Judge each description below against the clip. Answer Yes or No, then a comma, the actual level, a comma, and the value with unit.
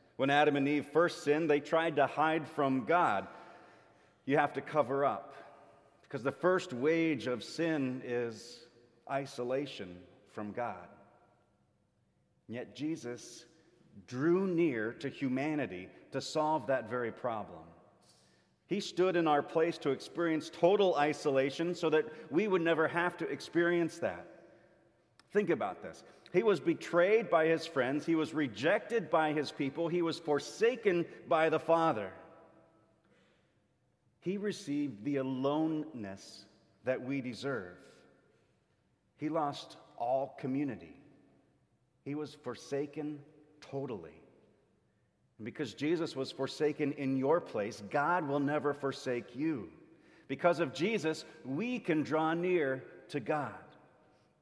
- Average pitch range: Yes, average, 3.8 semitones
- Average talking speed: No, slow, 125 wpm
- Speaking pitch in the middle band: Yes, medium, 145 Hz